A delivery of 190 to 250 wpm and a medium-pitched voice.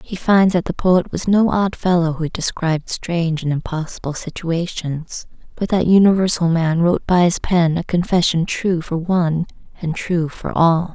No: average, 175 wpm; medium, 170 Hz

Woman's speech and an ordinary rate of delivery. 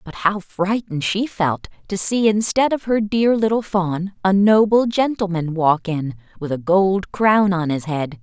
Yes: female; average, 180 wpm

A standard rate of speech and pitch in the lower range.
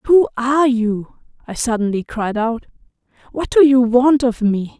No: average, 165 wpm; high, 245 Hz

